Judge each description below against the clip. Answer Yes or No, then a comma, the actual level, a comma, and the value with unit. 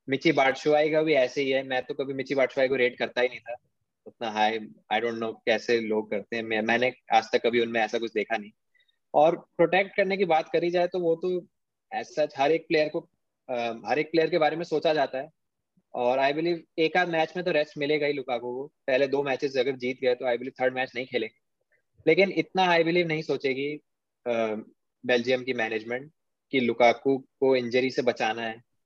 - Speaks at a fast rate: Yes, fast, 215 wpm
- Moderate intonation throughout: Yes, average, 4.5 semitones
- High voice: No, low, 135 Hz